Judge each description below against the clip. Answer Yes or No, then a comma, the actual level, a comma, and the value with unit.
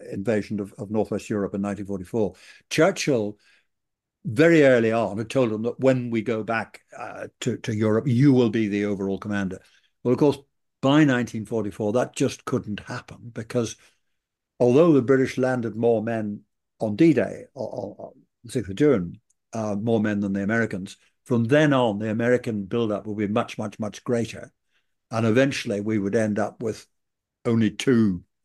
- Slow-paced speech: No, average, 170 wpm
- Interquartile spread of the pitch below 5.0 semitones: Yes, average, 3.0 semitones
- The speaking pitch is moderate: No, low, 115 Hz